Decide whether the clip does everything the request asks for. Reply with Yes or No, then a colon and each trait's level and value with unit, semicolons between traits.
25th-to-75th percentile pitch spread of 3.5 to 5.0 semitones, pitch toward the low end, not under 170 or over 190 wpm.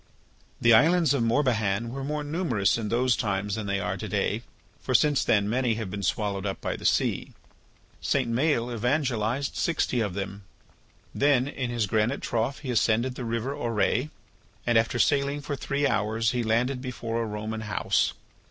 Yes: average, 3.8 semitones; low, 120 Hz; average, 175 wpm